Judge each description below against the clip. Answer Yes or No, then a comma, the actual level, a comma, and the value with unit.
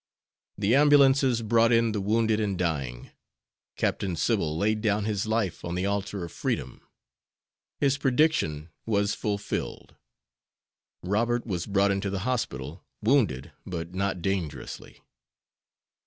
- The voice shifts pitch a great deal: No, average, 4.5 semitones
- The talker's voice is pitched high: No, low, 100 Hz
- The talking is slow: Yes, slow, 125 wpm